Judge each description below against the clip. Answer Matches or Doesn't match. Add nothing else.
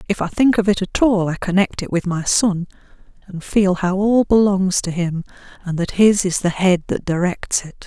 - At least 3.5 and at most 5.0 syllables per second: Matches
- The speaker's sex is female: Matches